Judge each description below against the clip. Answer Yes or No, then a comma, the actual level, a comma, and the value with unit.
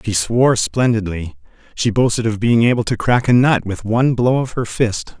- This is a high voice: No, low, 115 Hz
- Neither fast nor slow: No, fast, 210 wpm